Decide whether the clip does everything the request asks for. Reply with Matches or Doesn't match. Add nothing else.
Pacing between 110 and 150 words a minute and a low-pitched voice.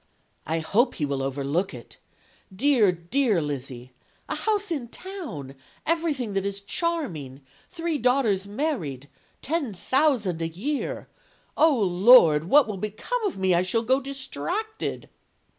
Doesn't match